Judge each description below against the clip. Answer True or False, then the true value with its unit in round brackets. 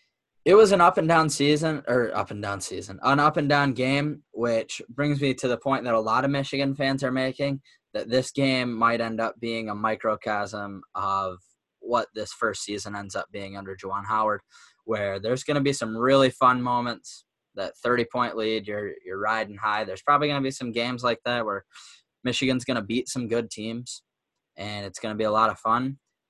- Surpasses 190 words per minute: True (200 wpm)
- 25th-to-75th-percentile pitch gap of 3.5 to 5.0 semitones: True (3.9 semitones)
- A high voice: False (120 Hz)